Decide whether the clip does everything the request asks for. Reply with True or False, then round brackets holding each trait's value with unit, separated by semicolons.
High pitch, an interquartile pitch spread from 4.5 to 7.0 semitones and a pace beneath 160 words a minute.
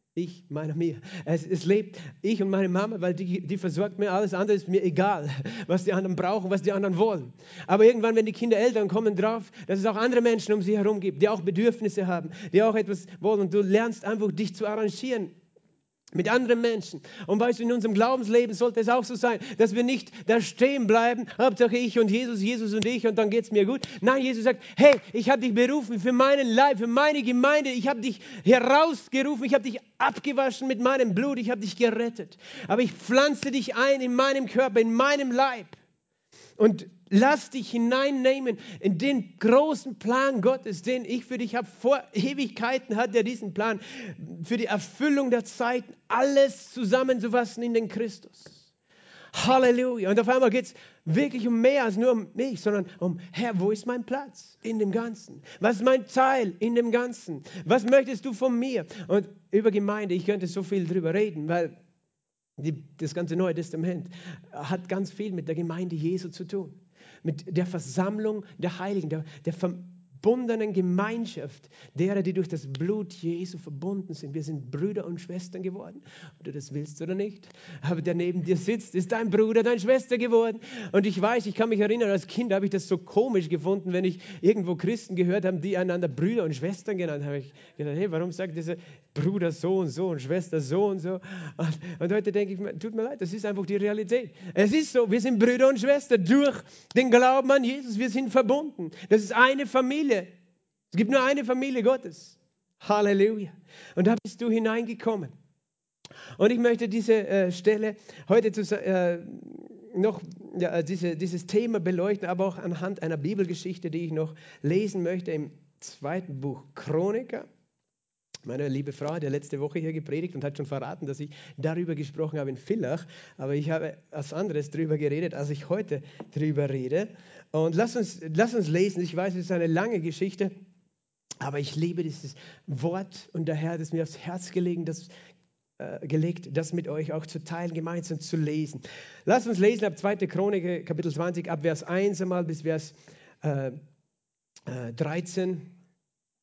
False (195 Hz; 5.2 semitones; 185 wpm)